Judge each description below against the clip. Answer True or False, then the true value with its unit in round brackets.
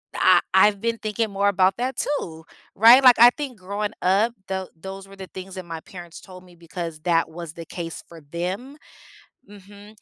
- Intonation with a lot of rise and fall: False (3.5 semitones)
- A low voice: False (190 Hz)